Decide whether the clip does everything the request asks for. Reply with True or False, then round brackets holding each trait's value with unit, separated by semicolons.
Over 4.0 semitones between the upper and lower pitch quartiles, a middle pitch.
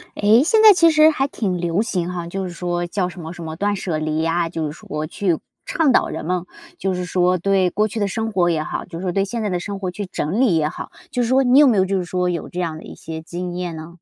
False (3.4 semitones; 180 Hz)